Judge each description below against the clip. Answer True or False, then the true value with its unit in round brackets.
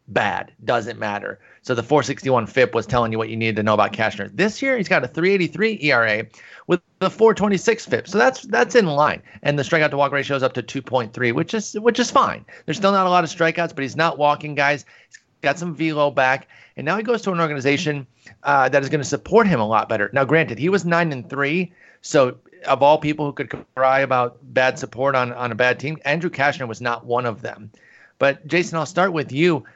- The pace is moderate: False (235 wpm)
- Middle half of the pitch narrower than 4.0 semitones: False (5.3 semitones)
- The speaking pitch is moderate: True (145 Hz)